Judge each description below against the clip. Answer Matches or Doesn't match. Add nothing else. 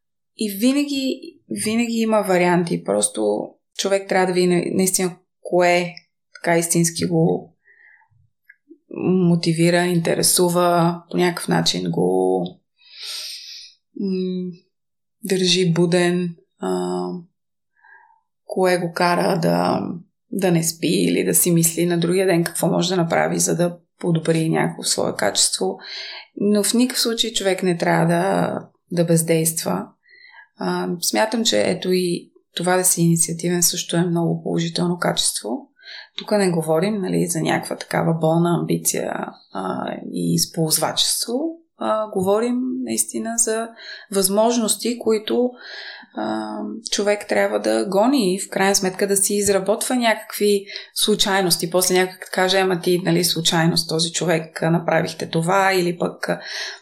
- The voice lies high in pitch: Doesn't match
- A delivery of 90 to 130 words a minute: Matches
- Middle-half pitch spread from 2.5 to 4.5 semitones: Matches